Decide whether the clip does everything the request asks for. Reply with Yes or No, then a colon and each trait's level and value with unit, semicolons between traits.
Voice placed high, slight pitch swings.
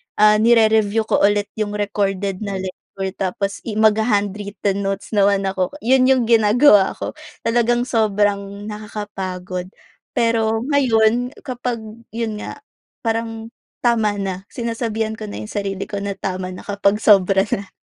Yes: high, 210 Hz; narrow, 2.2 semitones